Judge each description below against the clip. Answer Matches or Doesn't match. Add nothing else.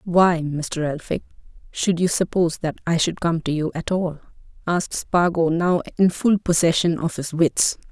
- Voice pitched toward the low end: Doesn't match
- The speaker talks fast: Doesn't match